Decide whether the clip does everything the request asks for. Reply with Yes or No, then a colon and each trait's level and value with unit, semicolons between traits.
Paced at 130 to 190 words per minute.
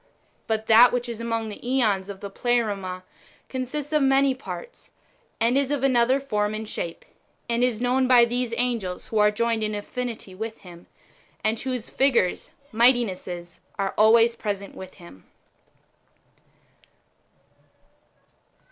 Yes: average, 140 wpm